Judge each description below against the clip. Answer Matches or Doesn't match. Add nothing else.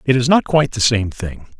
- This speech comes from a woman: Doesn't match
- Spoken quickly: Matches